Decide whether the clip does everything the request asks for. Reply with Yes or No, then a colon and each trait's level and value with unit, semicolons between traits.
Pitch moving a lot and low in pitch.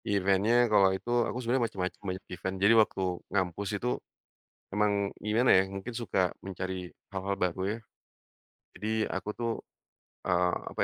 No: narrow, 2.4 semitones; low, 100 Hz